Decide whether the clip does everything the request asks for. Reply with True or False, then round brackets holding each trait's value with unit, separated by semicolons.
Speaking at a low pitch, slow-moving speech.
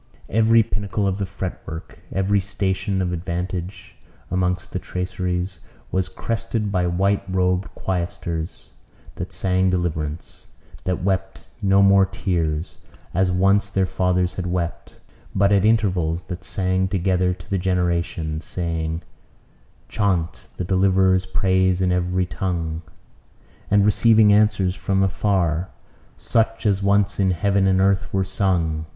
True (95 Hz; 130 wpm)